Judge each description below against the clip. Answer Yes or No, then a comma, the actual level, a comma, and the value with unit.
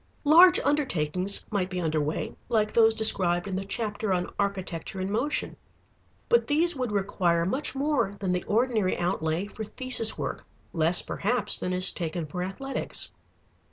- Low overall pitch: No, high, 200 Hz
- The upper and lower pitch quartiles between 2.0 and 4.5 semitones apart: No, average, 5.0 semitones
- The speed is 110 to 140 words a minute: No, average, 155 wpm